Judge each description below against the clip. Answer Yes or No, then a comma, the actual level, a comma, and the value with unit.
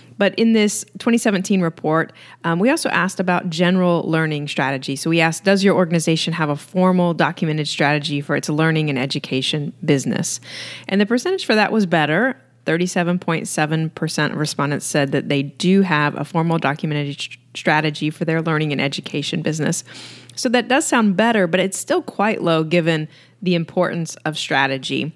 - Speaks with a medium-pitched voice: Yes, medium, 165 Hz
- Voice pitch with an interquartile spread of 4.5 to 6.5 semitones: No, average, 3.8 semitones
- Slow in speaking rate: No, average, 170 wpm